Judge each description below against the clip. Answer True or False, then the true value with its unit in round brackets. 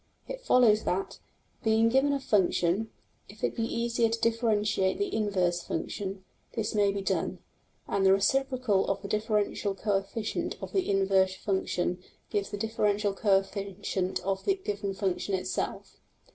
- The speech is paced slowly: False (150 wpm)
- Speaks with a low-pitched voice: False (205 Hz)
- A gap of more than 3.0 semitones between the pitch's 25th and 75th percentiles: False (2.7 semitones)